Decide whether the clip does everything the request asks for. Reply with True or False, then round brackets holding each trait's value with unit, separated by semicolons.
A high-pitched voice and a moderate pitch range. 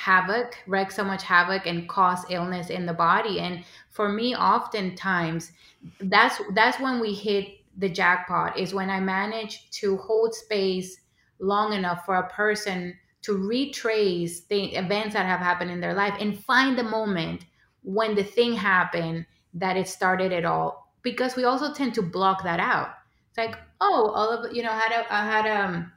True (195 Hz; 3.5 semitones)